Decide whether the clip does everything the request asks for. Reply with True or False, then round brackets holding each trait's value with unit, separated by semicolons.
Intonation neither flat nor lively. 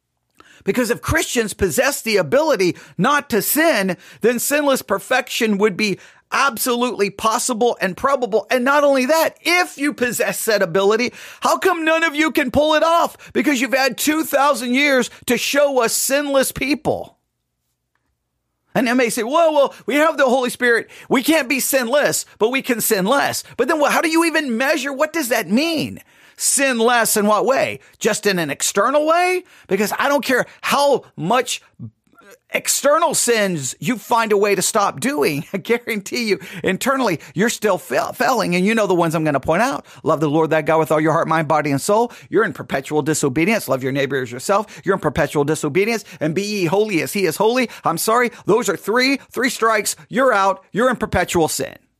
False (6.4 semitones)